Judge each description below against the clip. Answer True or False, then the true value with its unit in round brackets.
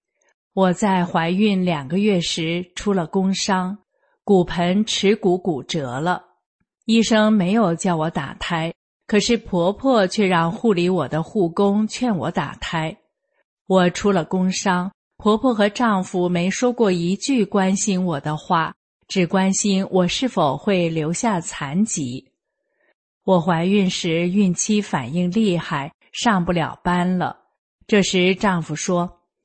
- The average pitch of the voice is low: False (185 Hz)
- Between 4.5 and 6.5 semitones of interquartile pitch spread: False (2.9 semitones)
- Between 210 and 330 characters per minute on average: False (190 characters per minute)